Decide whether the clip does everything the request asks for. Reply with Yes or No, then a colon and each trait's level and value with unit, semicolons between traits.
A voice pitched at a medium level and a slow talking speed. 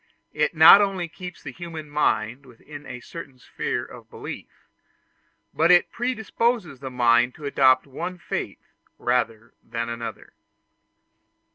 Yes: medium, 145 Hz; slow, 130 wpm